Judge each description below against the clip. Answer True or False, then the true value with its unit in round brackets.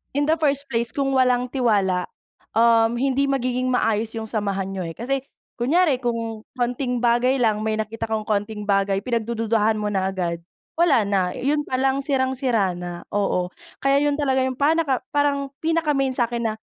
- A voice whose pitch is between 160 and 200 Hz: False (235 Hz)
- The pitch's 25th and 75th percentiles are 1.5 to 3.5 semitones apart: False (4.1 semitones)